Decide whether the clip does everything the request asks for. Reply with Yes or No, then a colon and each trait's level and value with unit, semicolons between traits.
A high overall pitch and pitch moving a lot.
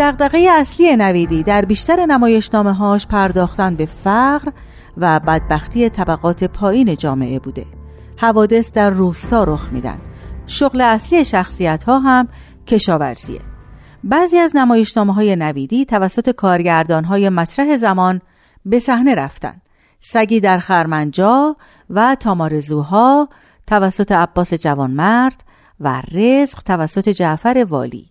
Yes: high, 205 Hz; wide, 6.4 semitones